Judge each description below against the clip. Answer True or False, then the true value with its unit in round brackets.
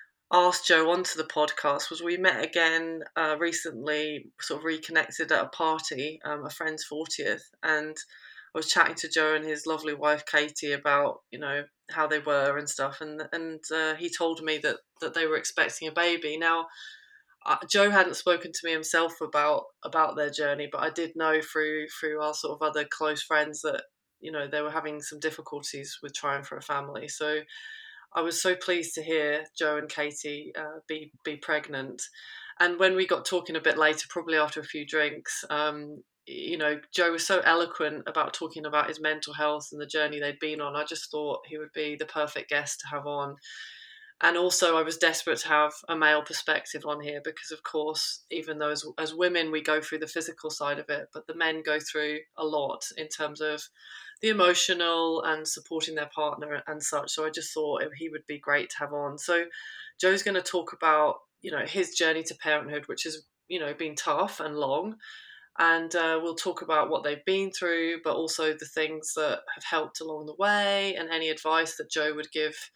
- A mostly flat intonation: True (1.7 semitones)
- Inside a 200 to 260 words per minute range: True (205 wpm)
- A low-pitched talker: False (155 Hz)